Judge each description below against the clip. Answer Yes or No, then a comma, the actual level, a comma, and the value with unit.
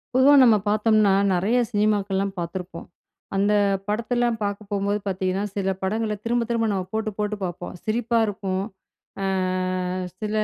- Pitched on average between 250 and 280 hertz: No, high, 210 Hz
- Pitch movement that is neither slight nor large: No, narrow, 2.3 semitones